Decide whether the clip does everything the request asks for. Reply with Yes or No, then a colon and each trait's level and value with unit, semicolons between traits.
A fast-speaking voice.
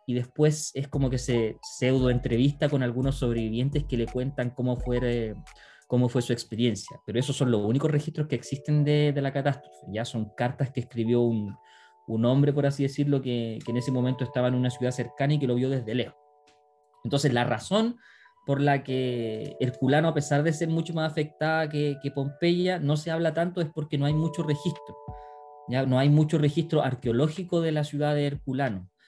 Yes: fast, 200 wpm